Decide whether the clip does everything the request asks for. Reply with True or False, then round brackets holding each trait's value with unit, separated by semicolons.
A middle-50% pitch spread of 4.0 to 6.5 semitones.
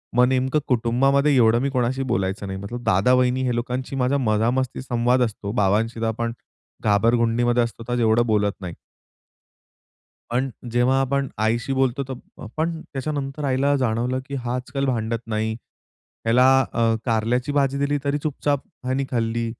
False (2.8 semitones)